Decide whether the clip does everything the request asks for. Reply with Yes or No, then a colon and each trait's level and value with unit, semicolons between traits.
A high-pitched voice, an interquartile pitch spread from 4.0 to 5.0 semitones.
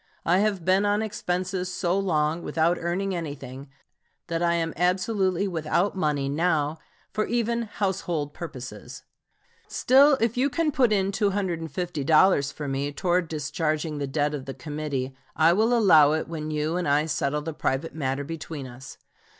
No: medium, 165 Hz; average, 4.4 semitones